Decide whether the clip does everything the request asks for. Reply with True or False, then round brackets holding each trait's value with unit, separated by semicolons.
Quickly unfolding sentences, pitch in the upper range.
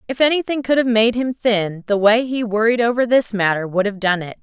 True (245 wpm; 225 Hz)